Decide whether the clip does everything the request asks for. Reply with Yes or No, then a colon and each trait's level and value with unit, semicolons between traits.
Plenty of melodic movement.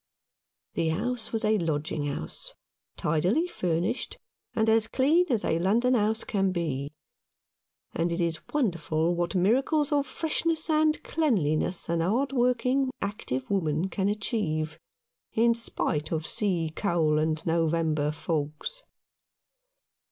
Yes: wide, 7.0 semitones